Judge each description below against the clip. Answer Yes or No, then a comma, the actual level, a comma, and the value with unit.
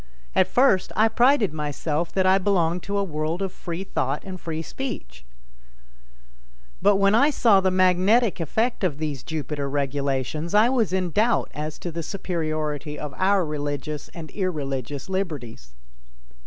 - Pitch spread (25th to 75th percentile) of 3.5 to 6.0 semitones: Yes, average, 4.7 semitones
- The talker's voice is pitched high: No, medium, 170 Hz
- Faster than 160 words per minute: No, average, 155 wpm